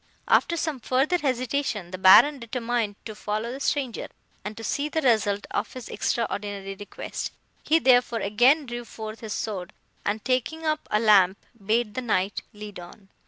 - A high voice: Yes, high, 230 Hz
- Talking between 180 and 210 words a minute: No, average, 165 wpm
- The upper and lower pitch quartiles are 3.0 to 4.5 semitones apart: Yes, average, 3.9 semitones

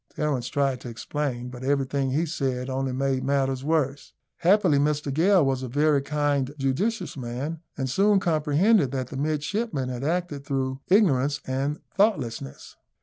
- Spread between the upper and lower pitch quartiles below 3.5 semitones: Yes, average, 2.9 semitones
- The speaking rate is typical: Yes, average, 150 wpm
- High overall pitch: No, medium, 140 Hz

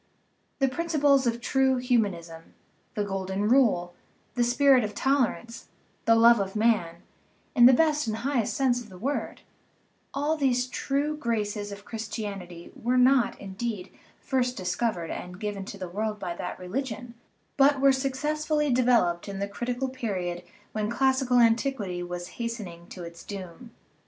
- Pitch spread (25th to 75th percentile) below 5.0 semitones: No, average, 5.3 semitones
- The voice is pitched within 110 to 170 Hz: No, high, 230 Hz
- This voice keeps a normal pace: Yes, average, 150 wpm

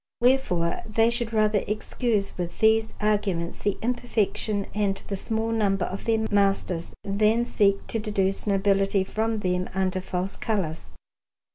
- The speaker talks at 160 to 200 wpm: No, average, 140 wpm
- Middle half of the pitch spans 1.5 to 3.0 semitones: Yes, narrow, 2.4 semitones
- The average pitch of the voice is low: No, high, 205 Hz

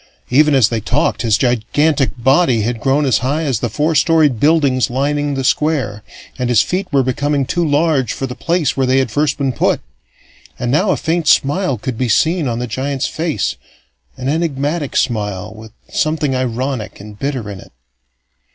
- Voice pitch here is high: No, low, 135 Hz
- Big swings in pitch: No, average, 3.6 semitones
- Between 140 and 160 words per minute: No, average, 185 wpm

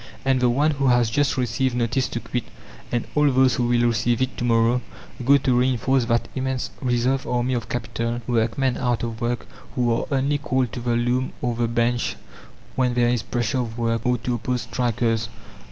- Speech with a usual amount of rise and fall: No, narrow, 1.7 semitones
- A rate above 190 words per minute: Yes, average, 200 wpm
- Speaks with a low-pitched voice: Yes, low, 120 Hz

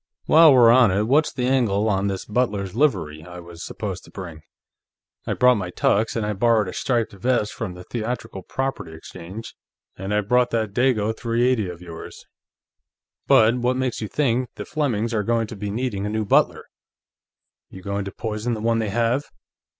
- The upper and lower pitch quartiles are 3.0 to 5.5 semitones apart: Yes, average, 3.8 semitones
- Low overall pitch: Yes, low, 110 Hz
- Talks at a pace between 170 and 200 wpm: Yes, average, 190 wpm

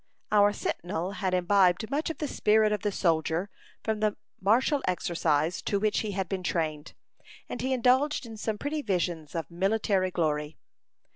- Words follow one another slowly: No, average, 165 wpm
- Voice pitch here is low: No, high, 195 Hz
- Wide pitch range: No, average, 4.1 semitones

